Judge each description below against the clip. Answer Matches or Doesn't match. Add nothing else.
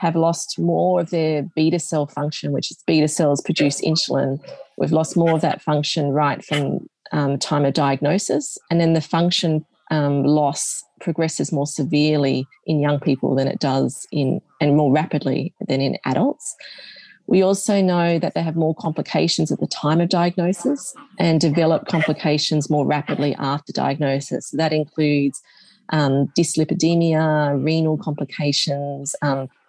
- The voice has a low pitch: Doesn't match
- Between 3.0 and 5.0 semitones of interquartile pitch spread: Doesn't match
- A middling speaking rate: Matches